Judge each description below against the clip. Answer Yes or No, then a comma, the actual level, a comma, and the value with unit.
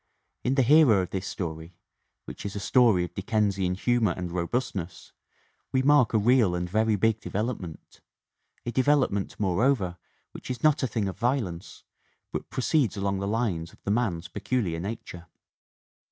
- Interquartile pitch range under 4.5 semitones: No, average, 5.2 semitones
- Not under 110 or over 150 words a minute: No, average, 165 wpm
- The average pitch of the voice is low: Yes, low, 105 Hz